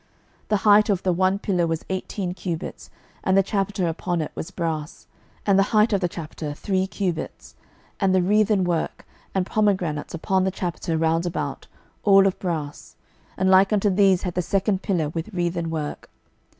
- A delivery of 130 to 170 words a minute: No, average, 180 wpm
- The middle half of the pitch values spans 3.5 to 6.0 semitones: No, average, 2.8 semitones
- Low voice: No, medium, 185 Hz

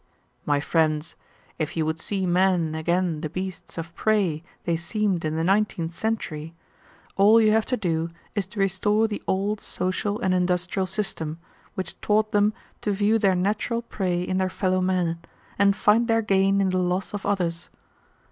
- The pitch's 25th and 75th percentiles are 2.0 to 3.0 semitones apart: No, average, 3.4 semitones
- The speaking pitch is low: No, medium, 185 Hz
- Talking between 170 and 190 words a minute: Yes, average, 175 wpm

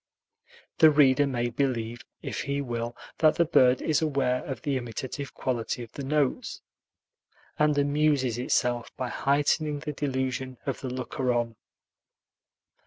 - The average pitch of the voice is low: Yes, low, 130 Hz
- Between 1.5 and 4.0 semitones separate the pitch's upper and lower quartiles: Yes, average, 2.9 semitones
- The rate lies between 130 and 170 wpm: Yes, average, 140 wpm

